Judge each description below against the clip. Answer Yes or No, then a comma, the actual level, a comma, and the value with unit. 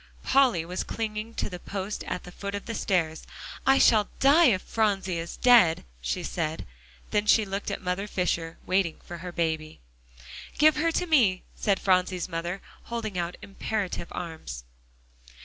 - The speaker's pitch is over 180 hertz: Yes, high, 190 Hz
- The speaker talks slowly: No, average, 165 wpm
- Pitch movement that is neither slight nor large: Yes, average, 4.2 semitones